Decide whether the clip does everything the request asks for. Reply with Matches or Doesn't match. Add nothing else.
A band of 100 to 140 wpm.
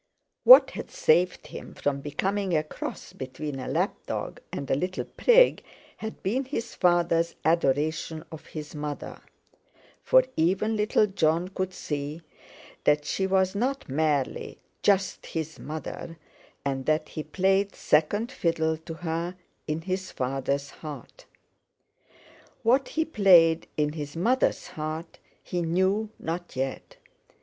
Matches